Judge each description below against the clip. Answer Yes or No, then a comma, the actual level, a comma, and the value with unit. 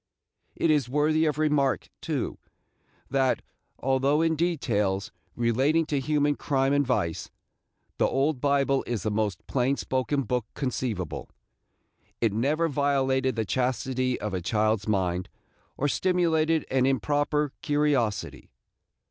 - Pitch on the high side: No, low, 135 Hz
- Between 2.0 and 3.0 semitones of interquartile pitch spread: No, average, 4.0 semitones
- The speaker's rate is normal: No, slow, 125 wpm